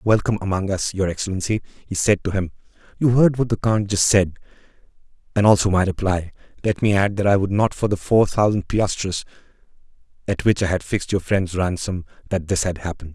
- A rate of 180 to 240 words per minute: Yes, average, 200 wpm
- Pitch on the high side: No, very low, 95 Hz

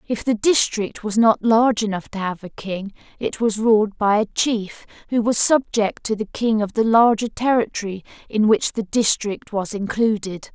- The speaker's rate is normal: Yes, average, 190 wpm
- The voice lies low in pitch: No, high, 215 Hz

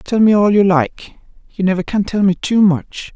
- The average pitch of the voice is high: Yes, high, 200 Hz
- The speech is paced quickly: Yes, fast, 230 wpm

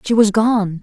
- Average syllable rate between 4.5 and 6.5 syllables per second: No, 4.1 syllables/s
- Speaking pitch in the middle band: No, high, 210 Hz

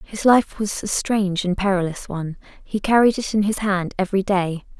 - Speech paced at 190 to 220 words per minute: Yes, average, 200 wpm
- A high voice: Yes, high, 195 Hz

